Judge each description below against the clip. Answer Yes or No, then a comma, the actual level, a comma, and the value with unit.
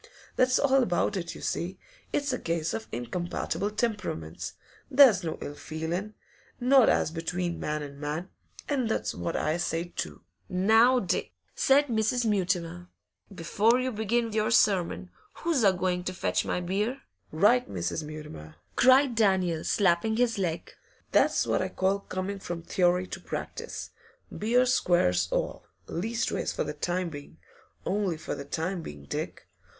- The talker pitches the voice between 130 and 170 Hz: No, medium, 185 Hz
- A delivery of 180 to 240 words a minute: No, average, 155 wpm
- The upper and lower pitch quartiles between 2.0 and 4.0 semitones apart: No, average, 5.3 semitones